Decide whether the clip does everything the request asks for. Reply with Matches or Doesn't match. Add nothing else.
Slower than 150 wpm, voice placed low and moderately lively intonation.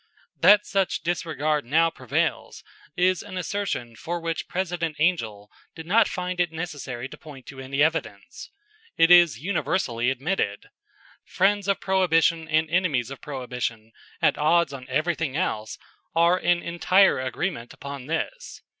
Doesn't match